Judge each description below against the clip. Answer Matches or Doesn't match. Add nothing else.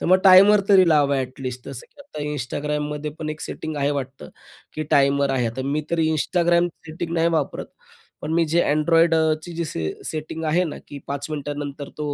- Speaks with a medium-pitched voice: Matches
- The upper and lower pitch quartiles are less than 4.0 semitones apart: Matches